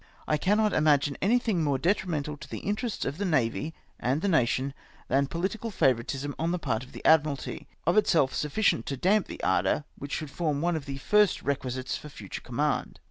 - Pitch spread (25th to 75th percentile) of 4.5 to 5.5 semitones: Yes, average, 4.9 semitones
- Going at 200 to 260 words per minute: Yes, fast, 205 wpm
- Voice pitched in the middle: Yes, medium, 150 Hz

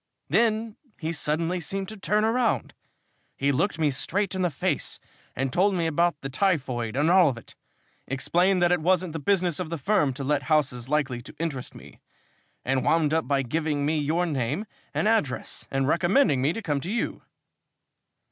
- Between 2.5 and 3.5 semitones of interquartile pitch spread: No, average, 4.9 semitones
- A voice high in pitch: No, medium, 160 Hz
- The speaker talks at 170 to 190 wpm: Yes, average, 185 wpm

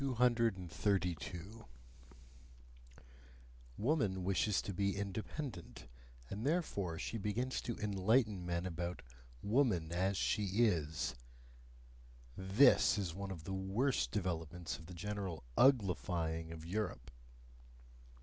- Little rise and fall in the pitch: No, average, 4.1 semitones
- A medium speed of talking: No, slow, 100 wpm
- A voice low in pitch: Yes, very low, 95 Hz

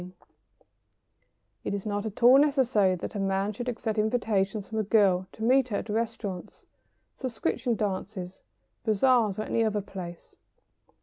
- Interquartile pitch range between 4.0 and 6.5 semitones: No, average, 3.0 semitones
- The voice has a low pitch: No, high, 215 Hz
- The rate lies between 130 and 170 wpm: Yes, average, 150 wpm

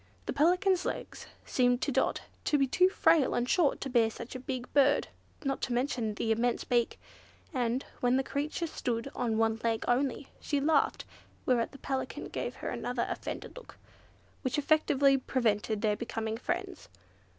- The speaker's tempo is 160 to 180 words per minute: Yes, average, 170 wpm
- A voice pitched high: Yes, very high, 255 Hz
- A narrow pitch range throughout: No, average, 3.6 semitones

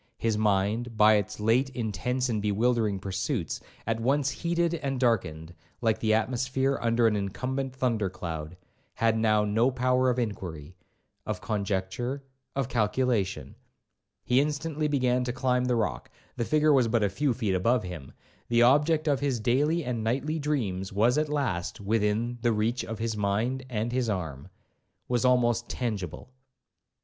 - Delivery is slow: No, average, 155 wpm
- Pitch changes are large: No, average, 3.8 semitones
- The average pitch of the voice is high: No, low, 115 Hz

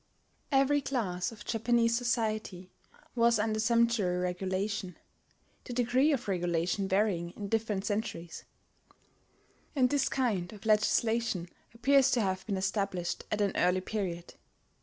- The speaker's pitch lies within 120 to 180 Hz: No, high, 215 Hz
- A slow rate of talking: Yes, slow, 125 wpm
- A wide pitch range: No, average, 3.9 semitones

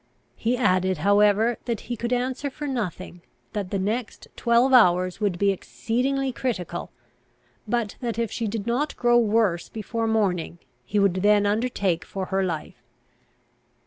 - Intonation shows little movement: No, average, 4.1 semitones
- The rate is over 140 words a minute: Yes, average, 150 wpm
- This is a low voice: No, high, 215 Hz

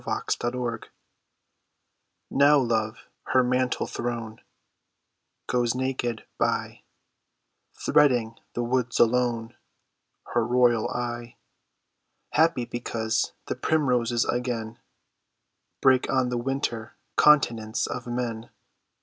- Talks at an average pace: No, slow, 95 wpm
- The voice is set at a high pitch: No, low, 120 Hz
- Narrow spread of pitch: Yes, narrow, 1.5 semitones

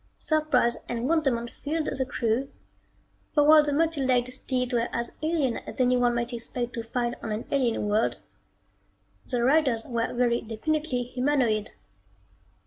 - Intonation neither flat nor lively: Yes, average, 3.4 semitones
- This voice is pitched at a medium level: No, very high, 250 Hz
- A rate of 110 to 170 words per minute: Yes, average, 145 wpm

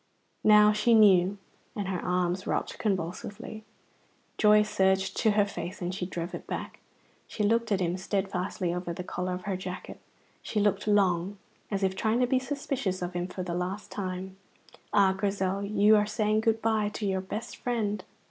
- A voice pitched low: No, high, 200 Hz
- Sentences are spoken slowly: No, average, 180 wpm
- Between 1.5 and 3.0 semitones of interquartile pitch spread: Yes, narrow, 2.4 semitones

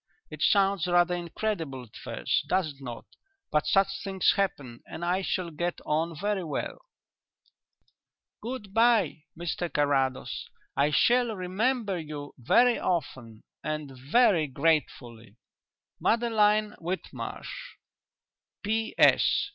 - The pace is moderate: No, slow, 110 wpm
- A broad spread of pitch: Yes, wide, 6.1 semitones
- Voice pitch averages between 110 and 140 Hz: No, medium, 175 Hz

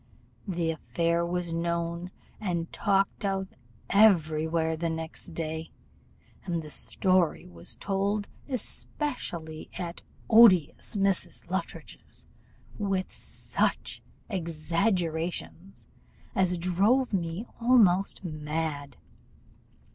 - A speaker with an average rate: No, slow, 90 wpm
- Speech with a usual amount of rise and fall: Yes, average, 3.1 semitones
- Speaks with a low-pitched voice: No, medium, 175 Hz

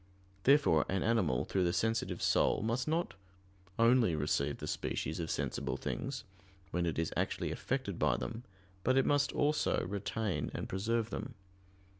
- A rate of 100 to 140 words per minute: No, average, 155 wpm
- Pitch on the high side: No, low, 110 Hz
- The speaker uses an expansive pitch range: Yes, wide, 6.6 semitones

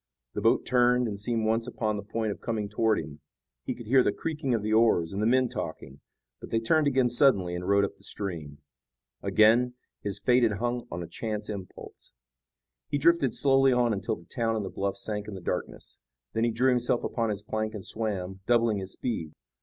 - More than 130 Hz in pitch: No, low, 110 Hz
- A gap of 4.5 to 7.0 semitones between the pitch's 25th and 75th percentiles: No, average, 3.4 semitones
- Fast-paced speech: Yes, fast, 215 wpm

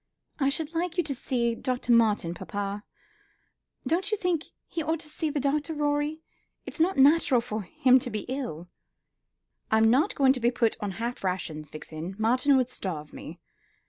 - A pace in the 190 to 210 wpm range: No, average, 175 wpm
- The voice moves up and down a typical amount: No, wide, 5.9 semitones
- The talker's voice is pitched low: No, very high, 255 Hz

